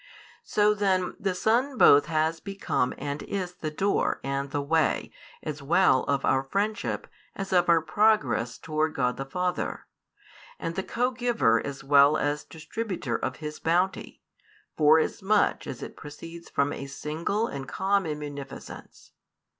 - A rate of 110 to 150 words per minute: Yes, average, 145 wpm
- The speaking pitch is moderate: Yes, medium, 160 Hz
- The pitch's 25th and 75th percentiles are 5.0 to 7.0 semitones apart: Yes, wide, 5.4 semitones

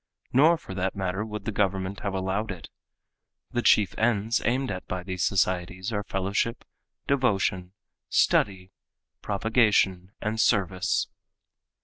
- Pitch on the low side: Yes, low, 100 Hz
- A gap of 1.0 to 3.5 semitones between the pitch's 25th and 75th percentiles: Yes, average, 3.1 semitones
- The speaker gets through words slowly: Yes, slow, 125 wpm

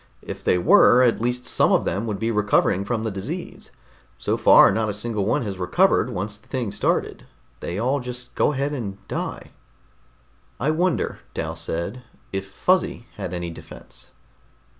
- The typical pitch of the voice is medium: No, low, 105 Hz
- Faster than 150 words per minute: Yes, average, 170 wpm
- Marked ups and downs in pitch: No, average, 4.2 semitones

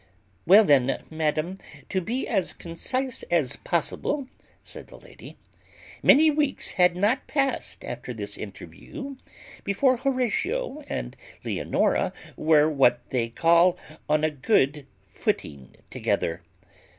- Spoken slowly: Yes, slow, 115 wpm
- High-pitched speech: No, medium, 180 Hz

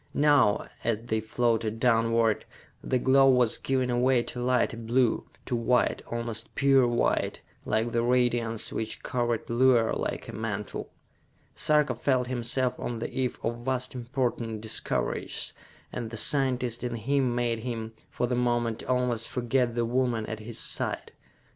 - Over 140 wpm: Yes, average, 150 wpm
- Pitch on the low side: Yes, low, 120 Hz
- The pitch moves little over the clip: Yes, narrow, 1.7 semitones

